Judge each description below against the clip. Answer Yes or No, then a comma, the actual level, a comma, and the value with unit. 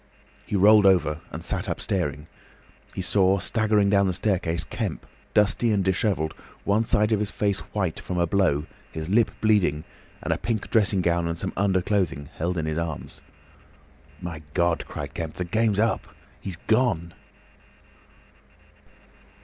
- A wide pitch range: No, average, 3.9 semitones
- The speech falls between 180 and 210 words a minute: No, average, 155 wpm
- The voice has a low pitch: Yes, very low, 95 Hz